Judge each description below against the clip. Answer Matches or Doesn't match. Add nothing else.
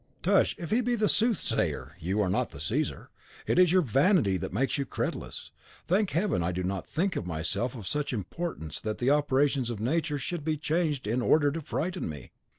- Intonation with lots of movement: Matches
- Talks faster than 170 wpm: Matches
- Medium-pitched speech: Matches